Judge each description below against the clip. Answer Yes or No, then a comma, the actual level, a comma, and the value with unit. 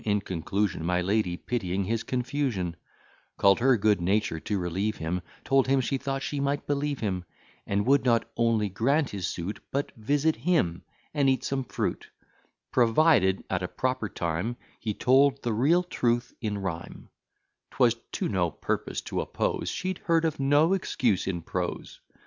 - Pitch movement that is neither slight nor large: No, wide, 6.3 semitones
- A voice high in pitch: No, low, 115 Hz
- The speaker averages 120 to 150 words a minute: No, average, 165 wpm